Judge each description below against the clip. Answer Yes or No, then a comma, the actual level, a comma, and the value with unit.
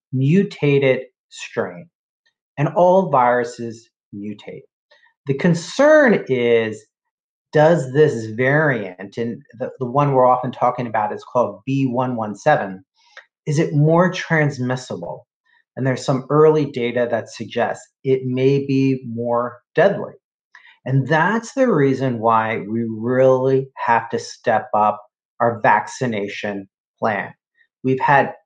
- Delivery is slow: Yes, slow, 115 wpm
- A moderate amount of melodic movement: Yes, average, 4.5 semitones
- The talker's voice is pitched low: Yes, low, 130 Hz